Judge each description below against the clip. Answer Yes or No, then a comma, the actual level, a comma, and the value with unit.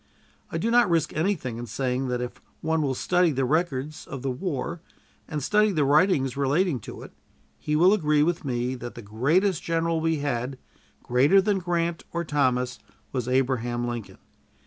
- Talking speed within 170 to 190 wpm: Yes, average, 175 wpm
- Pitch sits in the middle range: Yes, medium, 145 Hz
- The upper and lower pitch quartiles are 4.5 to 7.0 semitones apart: Yes, average, 5.1 semitones